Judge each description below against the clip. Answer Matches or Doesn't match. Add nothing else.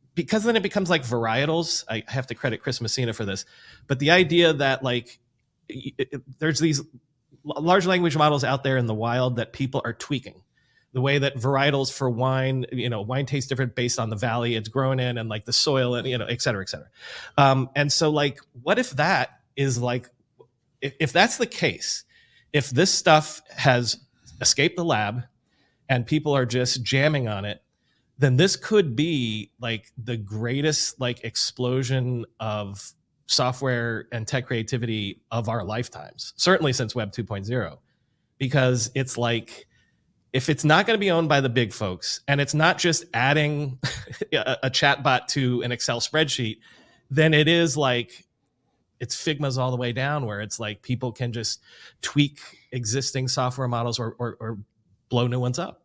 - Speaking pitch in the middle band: Doesn't match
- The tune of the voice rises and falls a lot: Doesn't match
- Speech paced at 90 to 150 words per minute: Doesn't match